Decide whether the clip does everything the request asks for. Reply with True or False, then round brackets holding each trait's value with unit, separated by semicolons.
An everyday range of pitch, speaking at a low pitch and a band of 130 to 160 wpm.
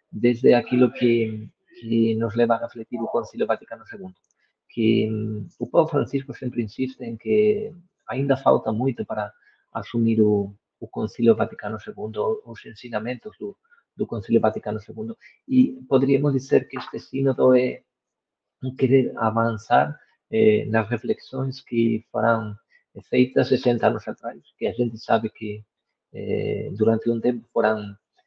True (3.1 semitones; 120 Hz; 135 wpm)